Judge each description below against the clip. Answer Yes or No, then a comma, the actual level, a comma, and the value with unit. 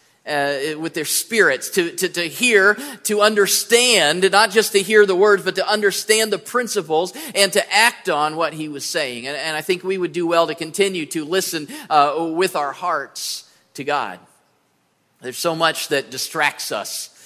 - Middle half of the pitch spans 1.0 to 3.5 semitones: No, average, 4.7 semitones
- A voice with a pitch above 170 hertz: Yes, high, 190 Hz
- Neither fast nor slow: Yes, average, 185 wpm